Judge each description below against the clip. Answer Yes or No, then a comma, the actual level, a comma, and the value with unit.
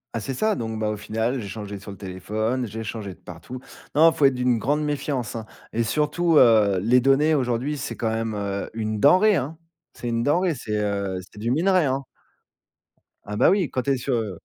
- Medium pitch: No, low, 120 Hz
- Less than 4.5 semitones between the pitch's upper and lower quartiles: No, average, 5.0 semitones